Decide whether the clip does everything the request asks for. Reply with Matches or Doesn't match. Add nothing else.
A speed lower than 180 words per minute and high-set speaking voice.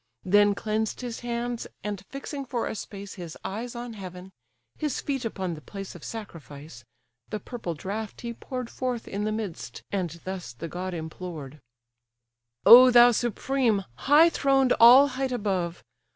Matches